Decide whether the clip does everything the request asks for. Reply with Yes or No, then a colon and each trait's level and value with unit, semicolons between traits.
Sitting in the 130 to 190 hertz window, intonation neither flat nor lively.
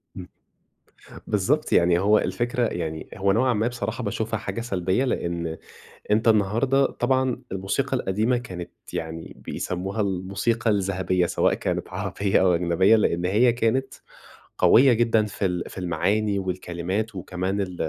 No: low, 100 Hz; average, 4.0 semitones